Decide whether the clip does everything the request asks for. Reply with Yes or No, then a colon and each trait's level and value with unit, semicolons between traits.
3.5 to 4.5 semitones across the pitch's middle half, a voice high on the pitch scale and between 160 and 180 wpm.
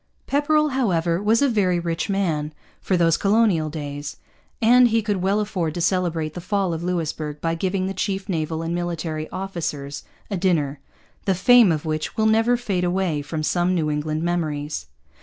No: average, 4.1 semitones; medium, 175 Hz; average, 175 wpm